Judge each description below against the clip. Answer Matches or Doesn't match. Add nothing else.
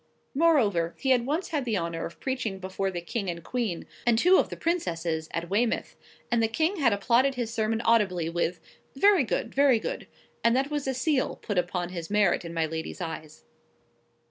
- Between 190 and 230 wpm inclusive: Matches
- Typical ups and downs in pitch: Doesn't match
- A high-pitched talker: Matches